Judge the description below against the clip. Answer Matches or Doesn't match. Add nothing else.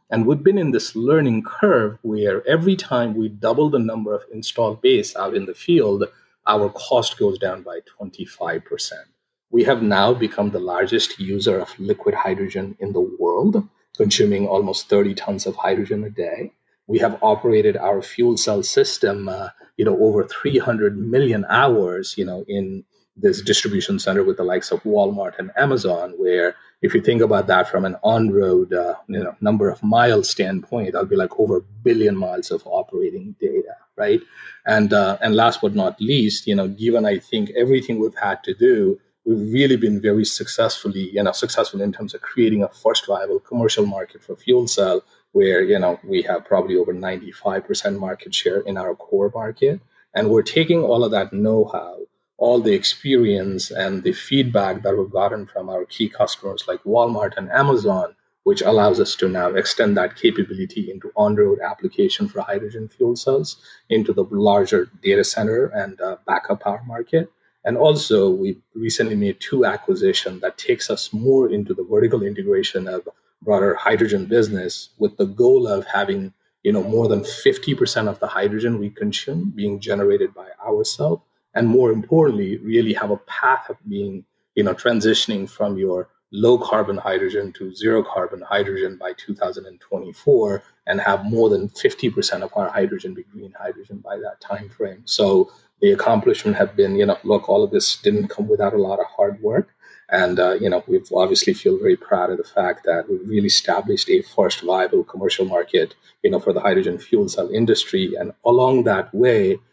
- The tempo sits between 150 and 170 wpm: Doesn't match